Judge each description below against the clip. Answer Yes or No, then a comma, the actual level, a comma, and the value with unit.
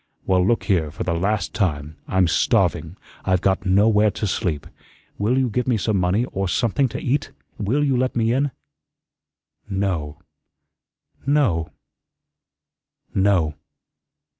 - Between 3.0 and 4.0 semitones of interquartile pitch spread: No, average, 4.8 semitones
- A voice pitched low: Yes, low, 100 Hz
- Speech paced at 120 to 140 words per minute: Yes, slow, 135 wpm